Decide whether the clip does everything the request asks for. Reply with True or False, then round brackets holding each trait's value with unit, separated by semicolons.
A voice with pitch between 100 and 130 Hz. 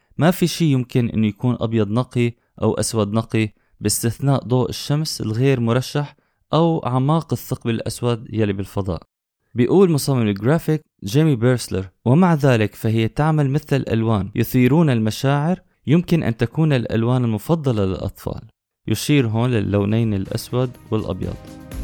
True (120 Hz)